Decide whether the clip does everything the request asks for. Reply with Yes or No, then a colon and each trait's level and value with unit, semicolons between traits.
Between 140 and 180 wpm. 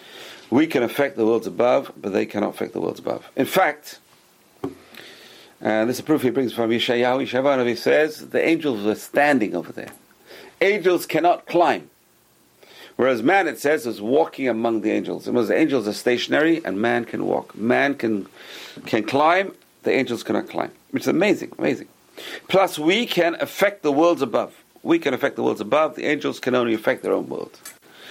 No: average, 190 wpm